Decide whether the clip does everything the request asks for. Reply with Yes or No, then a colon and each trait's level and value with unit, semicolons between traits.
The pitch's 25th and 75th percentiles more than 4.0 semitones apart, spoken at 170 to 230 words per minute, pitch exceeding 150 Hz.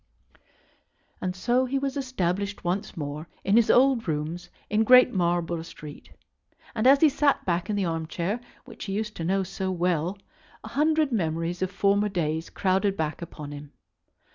Yes: average, 5.1 semitones; average, 175 wpm; high, 190 Hz